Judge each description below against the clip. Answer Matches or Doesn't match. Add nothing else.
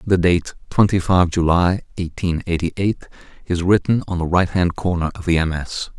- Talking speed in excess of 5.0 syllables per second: Doesn't match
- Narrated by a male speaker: Matches